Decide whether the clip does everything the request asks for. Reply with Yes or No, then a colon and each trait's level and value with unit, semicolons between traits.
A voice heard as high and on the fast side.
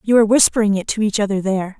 Yes: high, 210 Hz; fast, 265 wpm